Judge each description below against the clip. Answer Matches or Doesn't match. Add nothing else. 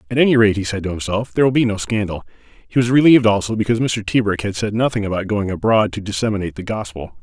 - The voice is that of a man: Matches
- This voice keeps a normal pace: Doesn't match